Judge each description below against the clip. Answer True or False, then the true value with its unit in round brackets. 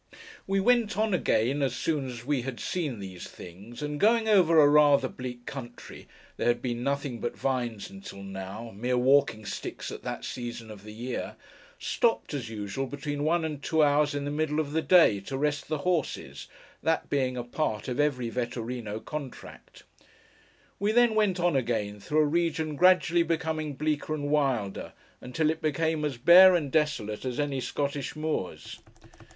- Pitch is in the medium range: True (145 Hz)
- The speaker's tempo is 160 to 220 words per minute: True (175 wpm)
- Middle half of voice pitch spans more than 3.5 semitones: True (4.7 semitones)